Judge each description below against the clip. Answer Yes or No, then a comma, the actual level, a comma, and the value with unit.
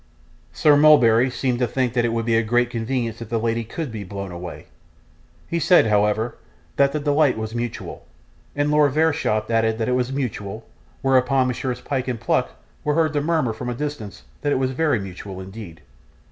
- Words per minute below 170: No, average, 195 wpm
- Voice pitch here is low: Yes, low, 120 Hz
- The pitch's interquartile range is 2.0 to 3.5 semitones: No, average, 4.2 semitones